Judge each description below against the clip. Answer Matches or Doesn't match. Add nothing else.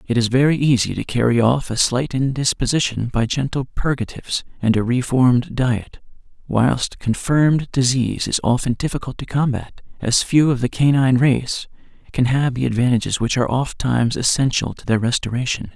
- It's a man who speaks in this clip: Matches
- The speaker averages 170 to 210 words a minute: Doesn't match